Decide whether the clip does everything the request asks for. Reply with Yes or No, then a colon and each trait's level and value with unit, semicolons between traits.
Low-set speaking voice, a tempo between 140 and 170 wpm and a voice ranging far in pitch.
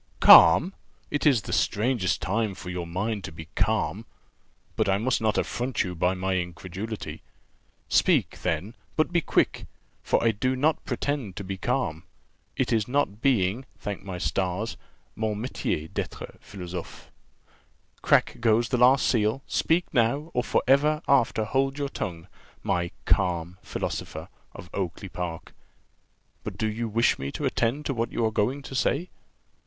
Yes: low, 110 Hz; average, 160 wpm; wide, 5.7 semitones